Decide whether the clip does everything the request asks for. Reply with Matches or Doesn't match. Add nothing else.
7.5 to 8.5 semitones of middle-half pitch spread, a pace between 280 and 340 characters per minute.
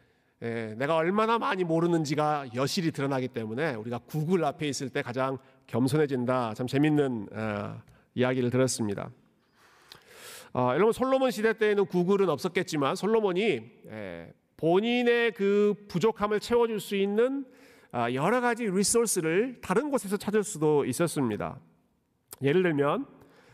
Matches